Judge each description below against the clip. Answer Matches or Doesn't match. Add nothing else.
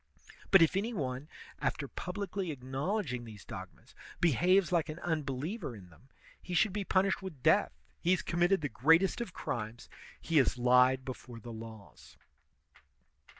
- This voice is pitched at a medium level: Matches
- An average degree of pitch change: Doesn't match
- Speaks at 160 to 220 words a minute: Doesn't match